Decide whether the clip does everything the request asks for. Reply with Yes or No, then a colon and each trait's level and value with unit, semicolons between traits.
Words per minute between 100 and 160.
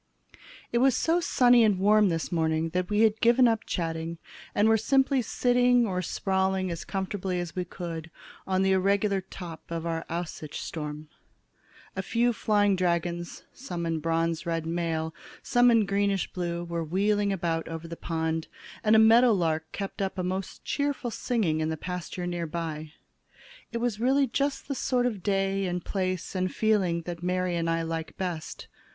No: average, 170 wpm